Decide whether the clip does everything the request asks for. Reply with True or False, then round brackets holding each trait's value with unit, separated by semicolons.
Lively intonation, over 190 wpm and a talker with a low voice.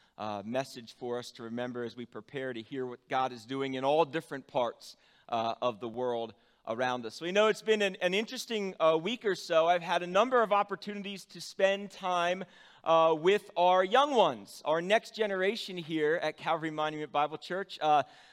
False (7.2 semitones; 200 wpm; 160 Hz)